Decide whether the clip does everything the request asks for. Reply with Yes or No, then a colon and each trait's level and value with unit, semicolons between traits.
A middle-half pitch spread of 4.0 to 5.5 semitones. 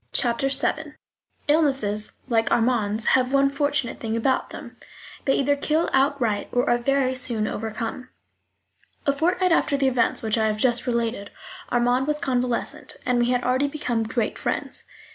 No: average, 3.3 semitones